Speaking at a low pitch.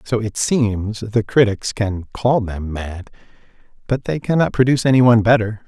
Yes: low, 110 Hz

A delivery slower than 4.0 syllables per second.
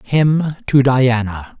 Yes: 3.2 syllables/s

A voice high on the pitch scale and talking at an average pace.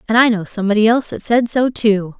No: high, 220 Hz; fast, 245 wpm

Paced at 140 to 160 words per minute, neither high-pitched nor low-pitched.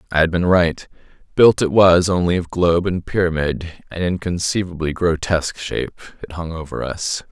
No: average, 155 wpm; very low, 85 Hz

